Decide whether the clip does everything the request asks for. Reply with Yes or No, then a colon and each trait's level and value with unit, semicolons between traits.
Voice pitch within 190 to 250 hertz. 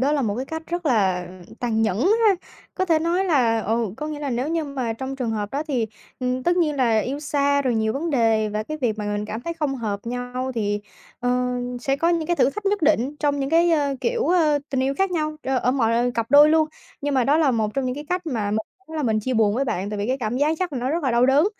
No: very high, 265 Hz